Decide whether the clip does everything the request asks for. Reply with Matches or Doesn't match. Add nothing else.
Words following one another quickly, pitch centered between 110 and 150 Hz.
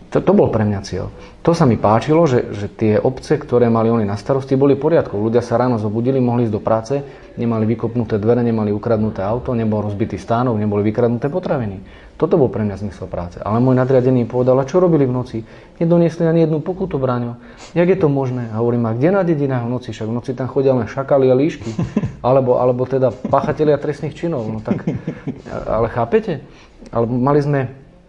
Matches